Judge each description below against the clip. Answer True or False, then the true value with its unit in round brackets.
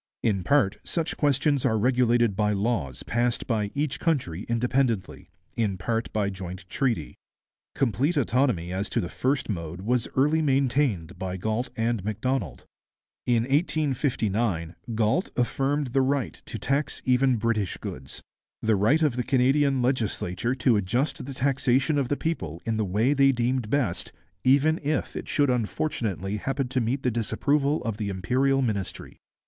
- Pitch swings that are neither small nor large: True (4.7 semitones)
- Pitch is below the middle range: True (120 Hz)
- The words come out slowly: False (155 wpm)